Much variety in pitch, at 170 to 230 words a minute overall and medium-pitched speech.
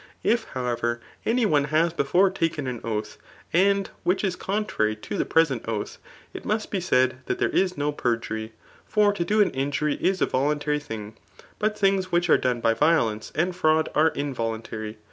Yes: wide, 7.8 semitones; average, 185 wpm; medium, 150 Hz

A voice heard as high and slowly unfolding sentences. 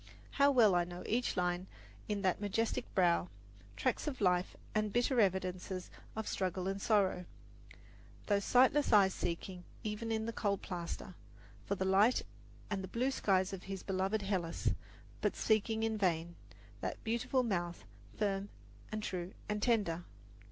No: high, 195 Hz; average, 150 wpm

